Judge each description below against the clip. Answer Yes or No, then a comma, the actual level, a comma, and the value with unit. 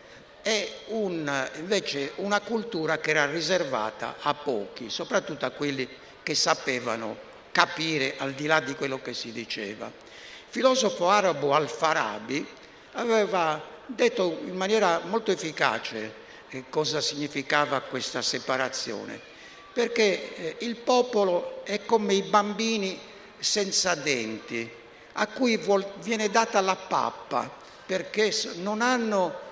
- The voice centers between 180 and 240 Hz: Yes, medium, 185 Hz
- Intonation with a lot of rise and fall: Yes, wide, 6.5 semitones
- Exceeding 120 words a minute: No, slow, 115 wpm